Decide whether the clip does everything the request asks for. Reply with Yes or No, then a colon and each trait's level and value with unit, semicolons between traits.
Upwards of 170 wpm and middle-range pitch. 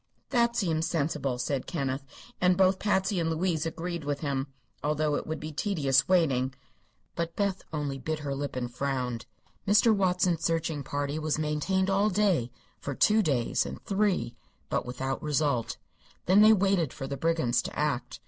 No: average, 165 wpm; medium, 155 Hz